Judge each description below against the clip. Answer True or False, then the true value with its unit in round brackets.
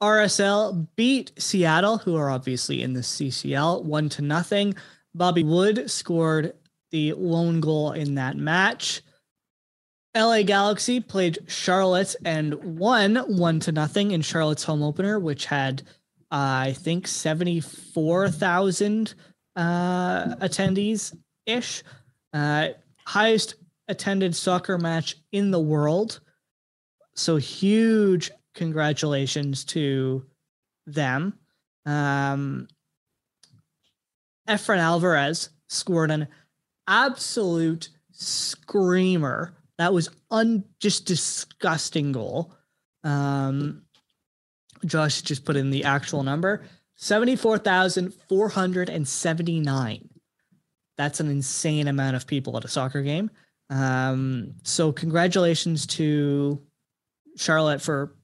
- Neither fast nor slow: False (100 wpm)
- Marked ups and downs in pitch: False (4.4 semitones)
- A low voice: False (165 Hz)